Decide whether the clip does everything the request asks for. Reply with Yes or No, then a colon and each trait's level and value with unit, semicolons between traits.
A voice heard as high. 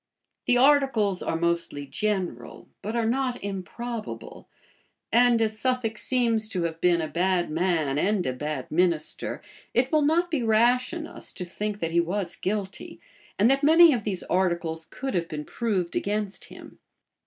Yes: high, 205 Hz